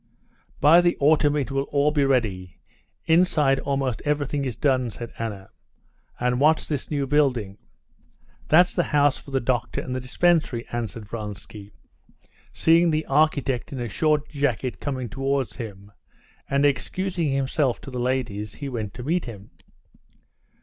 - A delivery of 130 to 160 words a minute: Yes, average, 150 wpm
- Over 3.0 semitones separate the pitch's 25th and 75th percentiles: Yes, average, 3.8 semitones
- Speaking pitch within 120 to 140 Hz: Yes, low, 135 Hz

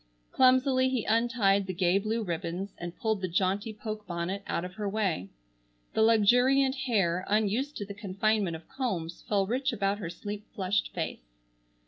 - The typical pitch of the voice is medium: No, high, 205 Hz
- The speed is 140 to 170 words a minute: Yes, average, 165 wpm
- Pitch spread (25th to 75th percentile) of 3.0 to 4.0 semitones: Yes, average, 3.6 semitones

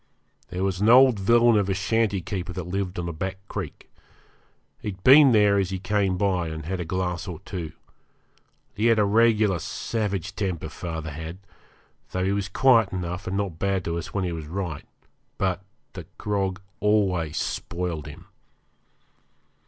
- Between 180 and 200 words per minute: No, average, 170 wpm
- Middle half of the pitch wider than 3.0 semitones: No, average, 2.7 semitones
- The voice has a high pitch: No, very low, 95 Hz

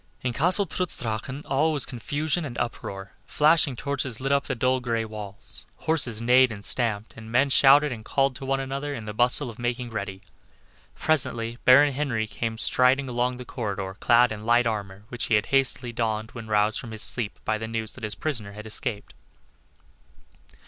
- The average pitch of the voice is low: Yes, low, 120 Hz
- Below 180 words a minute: No, average, 190 wpm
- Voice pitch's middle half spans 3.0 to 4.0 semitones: Yes, average, 3.7 semitones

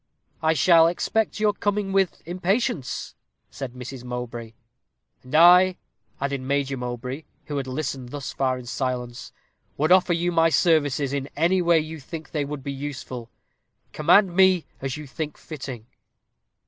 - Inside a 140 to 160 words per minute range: Yes, average, 150 wpm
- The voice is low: No, medium, 145 Hz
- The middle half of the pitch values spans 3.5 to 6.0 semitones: Yes, average, 4.8 semitones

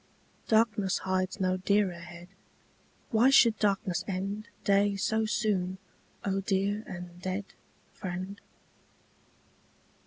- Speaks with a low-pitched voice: No, high, 195 Hz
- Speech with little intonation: Yes, narrow, 2.2 semitones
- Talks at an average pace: No, slow, 100 wpm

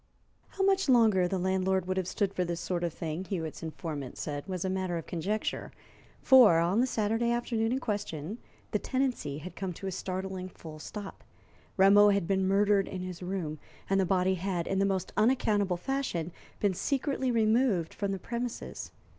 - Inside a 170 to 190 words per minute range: Yes, average, 180 wpm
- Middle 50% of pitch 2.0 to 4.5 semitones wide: Yes, average, 3.3 semitones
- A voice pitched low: No, high, 190 Hz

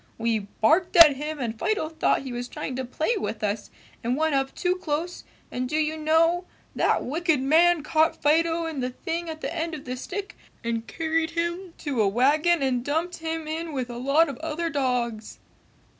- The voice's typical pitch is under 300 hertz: No, very high, 310 Hz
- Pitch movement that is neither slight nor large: Yes, average, 4.6 semitones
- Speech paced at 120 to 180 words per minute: No, average, 200 wpm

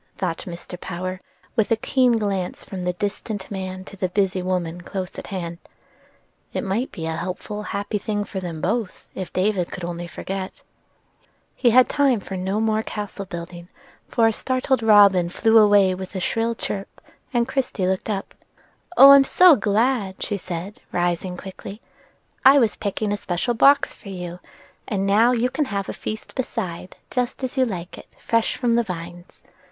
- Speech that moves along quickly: No, average, 180 wpm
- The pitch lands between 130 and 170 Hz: No, high, 200 Hz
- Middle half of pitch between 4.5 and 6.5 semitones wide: No, average, 3.8 semitones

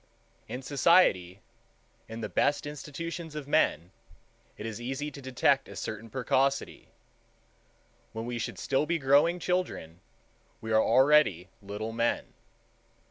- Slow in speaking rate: Yes, slow, 130 wpm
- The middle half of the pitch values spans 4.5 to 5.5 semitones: Yes, average, 5.0 semitones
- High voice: No, low, 135 Hz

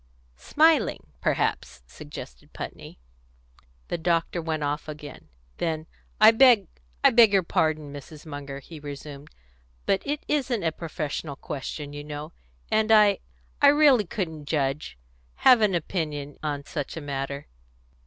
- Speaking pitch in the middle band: Yes, medium, 155 Hz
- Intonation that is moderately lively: No, wide, 6.1 semitones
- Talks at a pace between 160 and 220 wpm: No, slow, 135 wpm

